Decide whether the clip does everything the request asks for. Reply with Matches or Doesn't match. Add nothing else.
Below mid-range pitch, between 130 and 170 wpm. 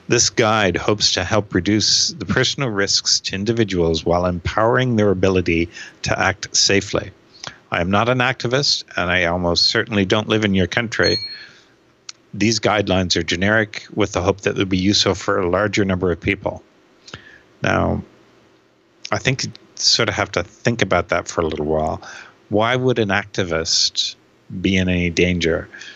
Matches